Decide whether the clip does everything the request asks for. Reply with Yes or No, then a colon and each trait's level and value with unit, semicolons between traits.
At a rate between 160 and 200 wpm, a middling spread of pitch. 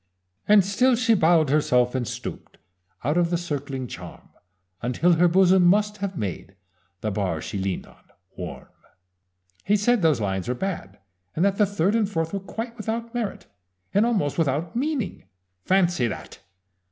No: average, 165 wpm; wide, 7.6 semitones